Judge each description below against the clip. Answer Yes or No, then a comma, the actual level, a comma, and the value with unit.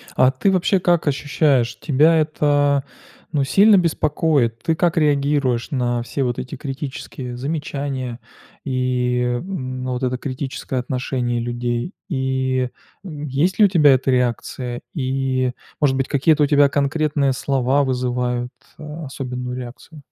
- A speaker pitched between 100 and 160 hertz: Yes, low, 135 Hz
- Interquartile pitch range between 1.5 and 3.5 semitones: Yes, average, 2.9 semitones